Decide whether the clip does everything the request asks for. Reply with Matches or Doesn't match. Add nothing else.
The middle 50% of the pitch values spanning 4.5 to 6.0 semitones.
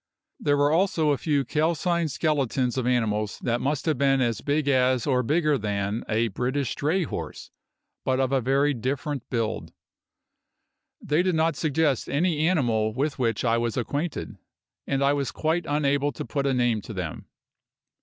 Doesn't match